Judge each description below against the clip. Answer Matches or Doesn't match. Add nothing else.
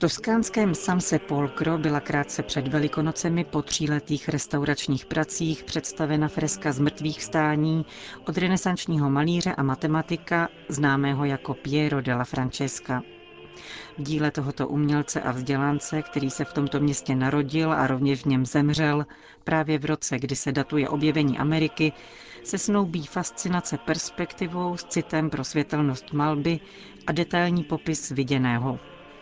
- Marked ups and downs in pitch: Doesn't match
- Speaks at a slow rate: Doesn't match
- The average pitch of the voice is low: Doesn't match